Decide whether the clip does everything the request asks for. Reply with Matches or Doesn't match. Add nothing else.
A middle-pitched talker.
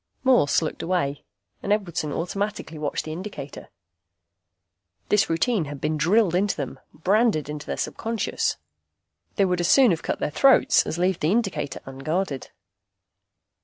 Matches